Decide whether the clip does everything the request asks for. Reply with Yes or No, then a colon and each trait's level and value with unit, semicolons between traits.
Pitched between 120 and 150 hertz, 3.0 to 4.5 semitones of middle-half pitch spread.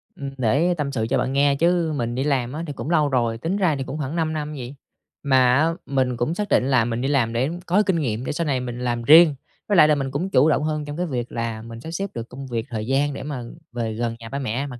Yes: low, 135 Hz; average, 4.1 semitones